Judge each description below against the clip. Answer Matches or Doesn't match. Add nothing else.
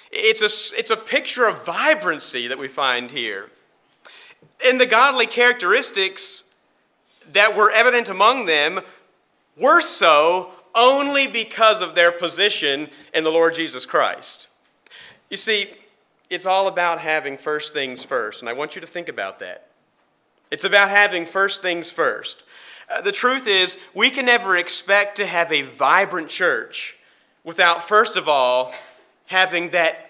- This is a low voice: Doesn't match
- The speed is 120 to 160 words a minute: Matches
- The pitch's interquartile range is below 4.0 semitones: Doesn't match